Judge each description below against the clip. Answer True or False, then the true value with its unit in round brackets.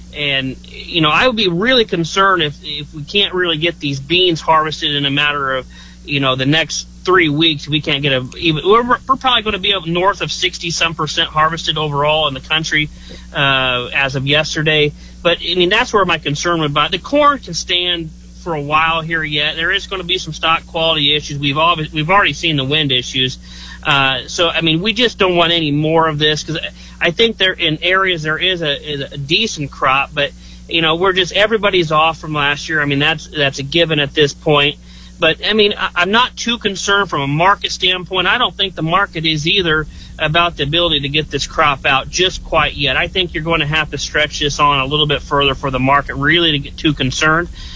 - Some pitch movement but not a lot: True (3.4 semitones)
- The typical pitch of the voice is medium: True (155 Hz)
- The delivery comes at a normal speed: False (235 wpm)